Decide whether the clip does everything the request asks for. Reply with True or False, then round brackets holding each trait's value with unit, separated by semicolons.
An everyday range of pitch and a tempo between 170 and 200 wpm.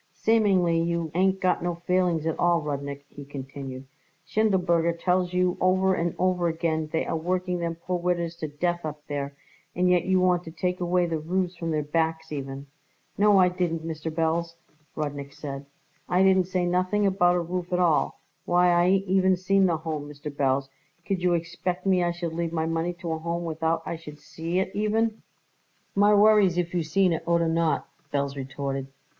False (2.3 semitones; 195 wpm)